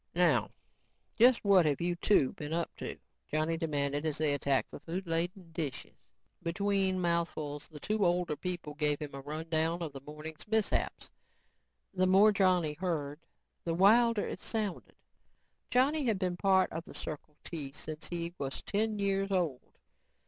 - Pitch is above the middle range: No, medium, 170 Hz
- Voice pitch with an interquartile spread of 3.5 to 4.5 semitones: Yes, average, 4.2 semitones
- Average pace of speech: Yes, average, 165 wpm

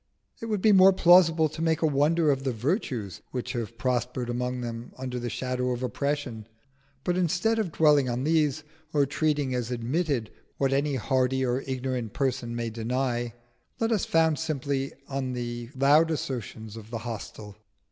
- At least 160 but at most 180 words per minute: Yes, average, 170 wpm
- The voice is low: Yes, low, 130 Hz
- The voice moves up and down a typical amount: Yes, average, 4.3 semitones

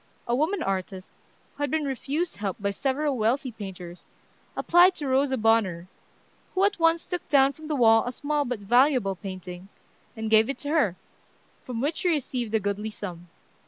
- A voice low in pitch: No, high, 245 Hz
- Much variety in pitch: Yes, wide, 6.4 semitones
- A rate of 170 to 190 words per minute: Yes, average, 180 wpm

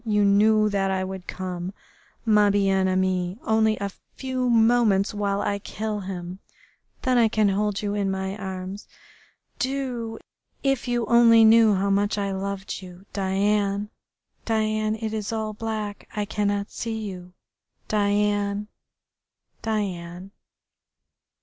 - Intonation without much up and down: Yes, narrow, 2.2 semitones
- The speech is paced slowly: Yes, slow, 130 wpm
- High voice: Yes, high, 205 Hz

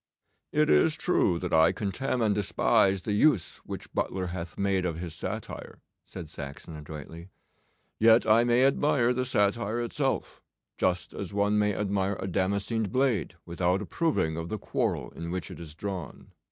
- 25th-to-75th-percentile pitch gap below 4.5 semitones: No, average, 4.8 semitones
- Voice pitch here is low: Yes, low, 100 Hz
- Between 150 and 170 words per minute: Yes, average, 165 wpm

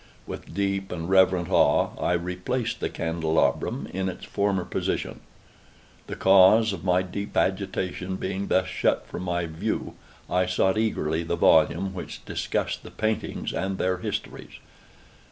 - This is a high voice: No, very low, 95 Hz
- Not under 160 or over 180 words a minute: No, average, 140 wpm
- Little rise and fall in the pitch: Yes, narrow, 1.5 semitones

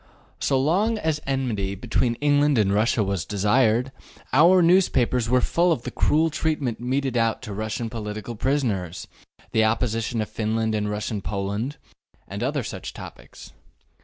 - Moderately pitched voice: No, low, 120 Hz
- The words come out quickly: No, average, 150 wpm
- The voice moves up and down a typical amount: Yes, average, 4.8 semitones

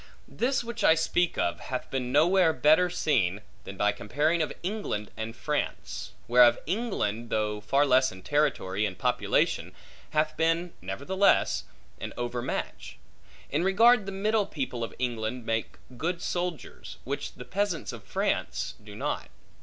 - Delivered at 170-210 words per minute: No, average, 145 wpm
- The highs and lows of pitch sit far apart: Yes, wide, 7.4 semitones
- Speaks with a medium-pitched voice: Yes, medium, 145 Hz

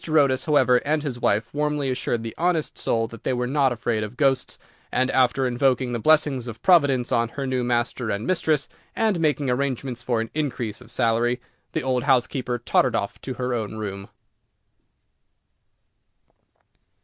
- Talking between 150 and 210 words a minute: Yes, average, 165 wpm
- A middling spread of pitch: Yes, average, 3.0 semitones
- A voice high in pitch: No, low, 125 Hz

